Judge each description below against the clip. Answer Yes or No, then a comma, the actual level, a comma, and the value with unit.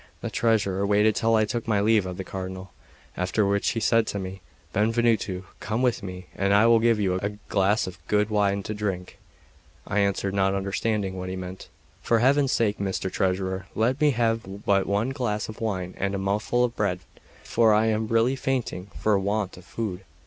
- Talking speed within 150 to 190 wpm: No, average, 200 wpm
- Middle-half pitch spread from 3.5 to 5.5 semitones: No, average, 2.8 semitones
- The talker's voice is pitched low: Yes, low, 105 Hz